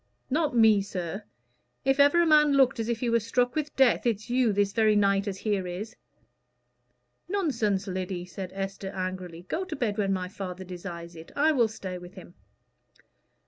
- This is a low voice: No, high, 205 Hz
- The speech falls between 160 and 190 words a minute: Yes, average, 185 wpm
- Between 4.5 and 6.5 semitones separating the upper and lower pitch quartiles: Yes, average, 4.9 semitones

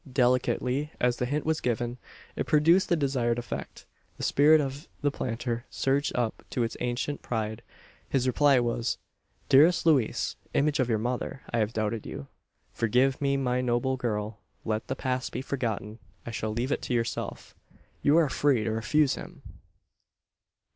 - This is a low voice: Yes, low, 125 Hz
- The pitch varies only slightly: No, average, 3.3 semitones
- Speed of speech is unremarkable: Yes, average, 165 wpm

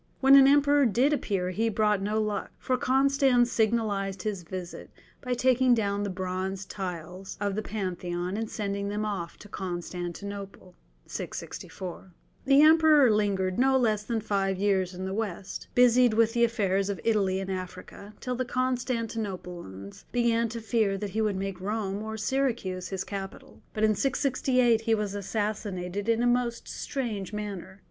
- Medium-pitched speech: No, high, 210 Hz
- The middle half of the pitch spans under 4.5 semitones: Yes, average, 3.6 semitones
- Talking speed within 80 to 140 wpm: No, average, 160 wpm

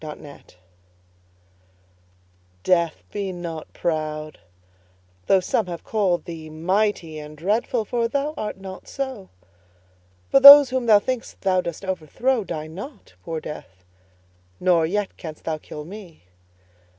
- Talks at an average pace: No, slow, 125 wpm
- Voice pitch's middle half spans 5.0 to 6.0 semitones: Yes, wide, 5.4 semitones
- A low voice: No, medium, 185 Hz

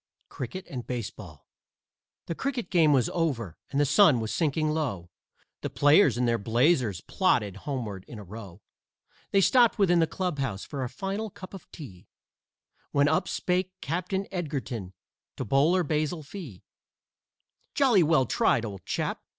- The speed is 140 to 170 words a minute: Yes, average, 150 wpm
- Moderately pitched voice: Yes, medium, 145 Hz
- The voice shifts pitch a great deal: Yes, wide, 7.6 semitones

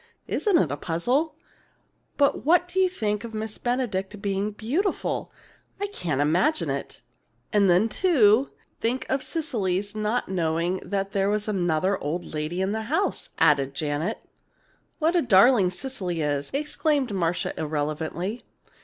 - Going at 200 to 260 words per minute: No, average, 140 wpm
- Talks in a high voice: Yes, high, 205 Hz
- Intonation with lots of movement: Yes, wide, 7.1 semitones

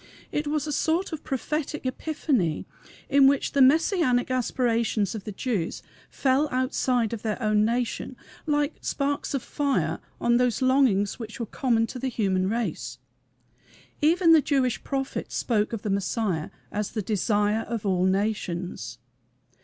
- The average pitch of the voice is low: No, high, 240 Hz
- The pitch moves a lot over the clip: No, average, 4.9 semitones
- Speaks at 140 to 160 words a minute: Yes, average, 150 wpm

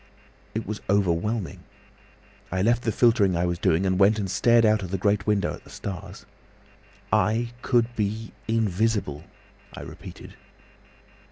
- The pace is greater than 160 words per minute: No, average, 150 wpm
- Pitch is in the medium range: No, low, 105 Hz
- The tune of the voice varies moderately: Yes, average, 3.2 semitones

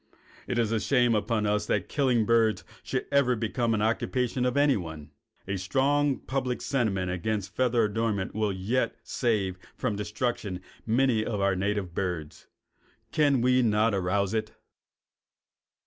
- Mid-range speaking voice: No, low, 110 Hz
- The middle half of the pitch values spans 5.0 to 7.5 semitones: No, average, 3.9 semitones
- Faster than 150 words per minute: No, average, 145 wpm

